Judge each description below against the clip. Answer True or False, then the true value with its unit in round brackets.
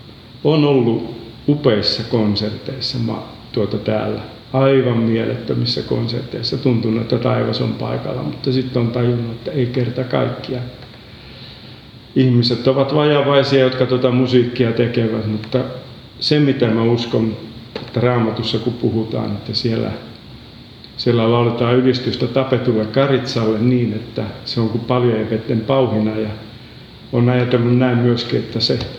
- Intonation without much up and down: True (2.2 semitones)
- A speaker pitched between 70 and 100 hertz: False (120 Hz)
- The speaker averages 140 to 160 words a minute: False (125 wpm)